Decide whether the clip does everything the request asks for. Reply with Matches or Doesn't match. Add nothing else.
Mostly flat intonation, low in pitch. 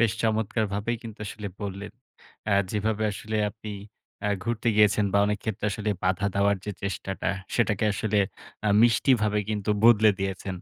Matches